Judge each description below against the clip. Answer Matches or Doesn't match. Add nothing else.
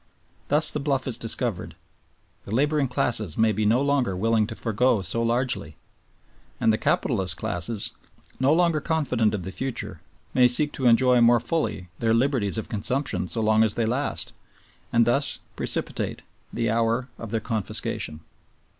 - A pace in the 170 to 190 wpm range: Doesn't match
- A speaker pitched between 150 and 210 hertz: Doesn't match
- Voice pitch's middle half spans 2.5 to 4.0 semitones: Matches